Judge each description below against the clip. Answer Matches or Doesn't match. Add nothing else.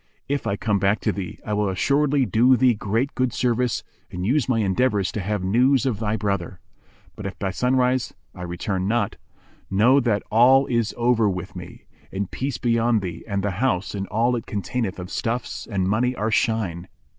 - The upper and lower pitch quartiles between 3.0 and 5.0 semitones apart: Matches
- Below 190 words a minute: Doesn't match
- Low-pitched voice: Matches